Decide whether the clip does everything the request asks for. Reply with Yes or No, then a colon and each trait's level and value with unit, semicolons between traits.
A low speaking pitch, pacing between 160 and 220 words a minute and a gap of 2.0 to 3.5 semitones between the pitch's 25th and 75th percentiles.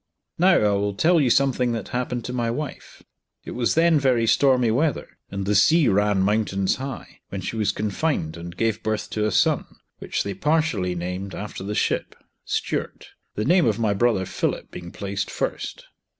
No: low, 110 Hz; average, 185 wpm; average, 4.8 semitones